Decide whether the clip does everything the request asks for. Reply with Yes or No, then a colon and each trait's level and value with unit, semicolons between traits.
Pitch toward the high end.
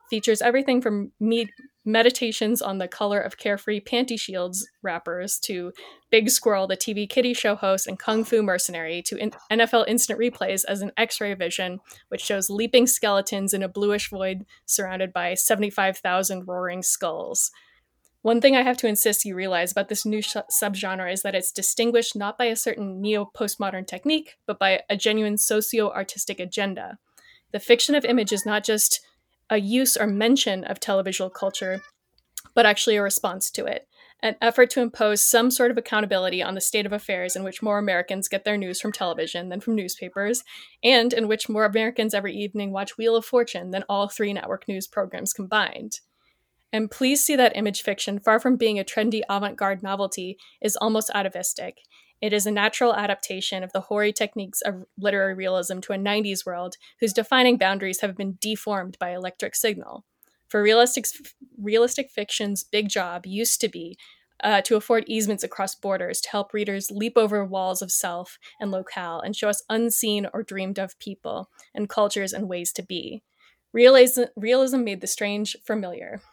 Yes: high, 210 Hz